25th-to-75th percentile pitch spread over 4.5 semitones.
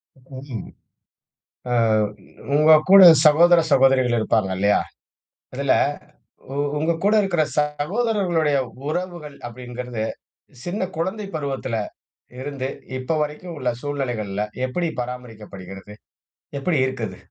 Yes: average, 5.1 semitones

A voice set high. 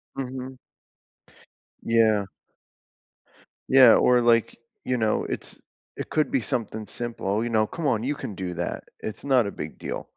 No: low, 115 Hz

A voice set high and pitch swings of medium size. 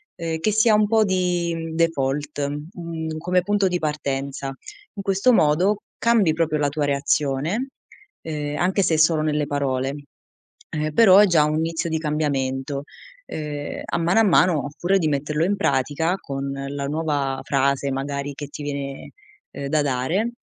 No: medium, 155 Hz; average, 3.8 semitones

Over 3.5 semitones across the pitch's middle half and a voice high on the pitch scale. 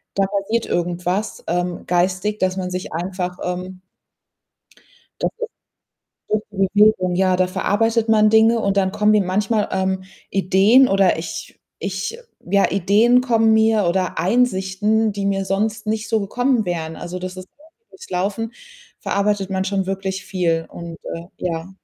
No: average, 2.8 semitones; high, 195 Hz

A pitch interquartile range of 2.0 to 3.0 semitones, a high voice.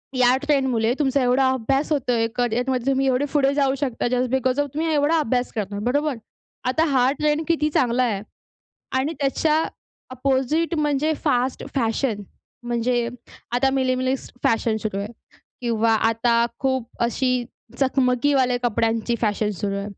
Yes: average, 2.7 semitones; very high, 255 Hz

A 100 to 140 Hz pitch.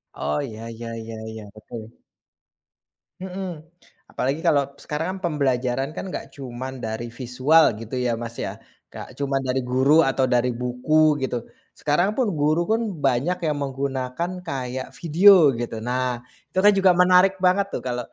Yes: low, 135 Hz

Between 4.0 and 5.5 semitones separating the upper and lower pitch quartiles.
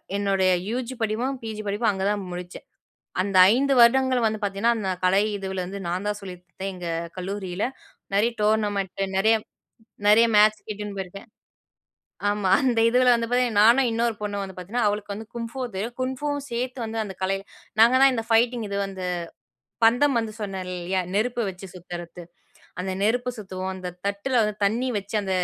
No: average, 3.5 semitones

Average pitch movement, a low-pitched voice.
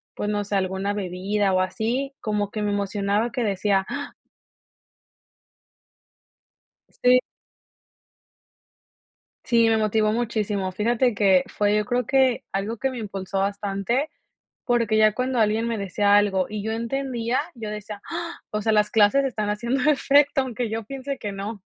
No: average, 3.0 semitones; high, 215 Hz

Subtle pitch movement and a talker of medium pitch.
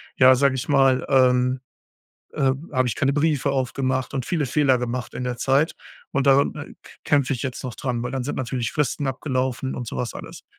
No: narrow, 1.6 semitones; low, 130 Hz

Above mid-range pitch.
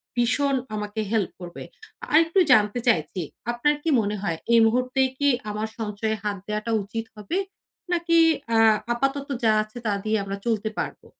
Yes: high, 220 Hz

